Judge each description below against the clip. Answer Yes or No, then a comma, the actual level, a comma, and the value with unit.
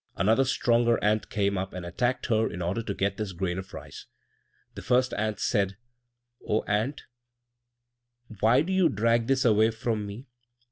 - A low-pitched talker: Yes, low, 110 Hz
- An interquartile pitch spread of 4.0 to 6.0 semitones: No, average, 3.2 semitones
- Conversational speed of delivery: Yes, average, 170 wpm